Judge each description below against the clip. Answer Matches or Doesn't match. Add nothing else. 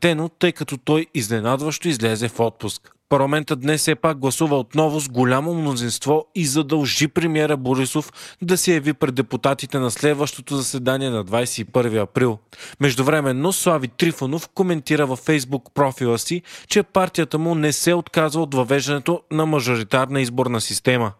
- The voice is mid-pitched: Matches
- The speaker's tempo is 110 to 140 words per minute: Doesn't match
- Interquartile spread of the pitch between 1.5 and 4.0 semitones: Matches